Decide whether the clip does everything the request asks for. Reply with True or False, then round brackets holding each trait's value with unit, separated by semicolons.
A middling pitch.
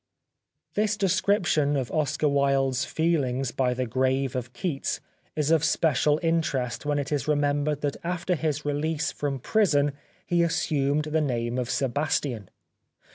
True (145 Hz)